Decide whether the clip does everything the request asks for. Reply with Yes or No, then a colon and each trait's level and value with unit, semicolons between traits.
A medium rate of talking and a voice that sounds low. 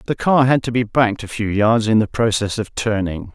No: fast, 250 wpm; low, 110 Hz